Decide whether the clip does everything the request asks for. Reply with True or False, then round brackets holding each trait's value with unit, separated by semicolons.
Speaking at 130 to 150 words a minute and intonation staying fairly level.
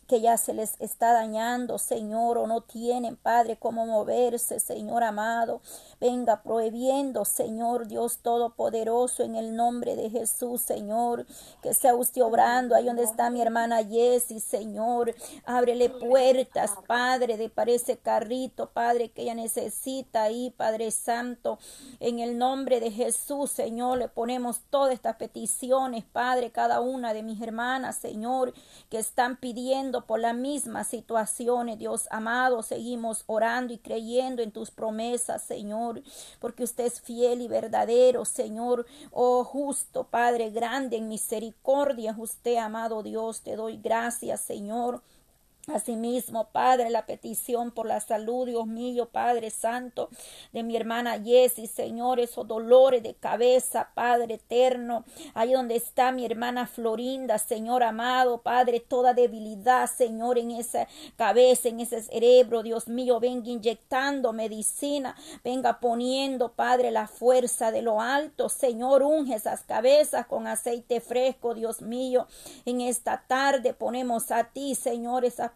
True (140 wpm; 1.7 semitones)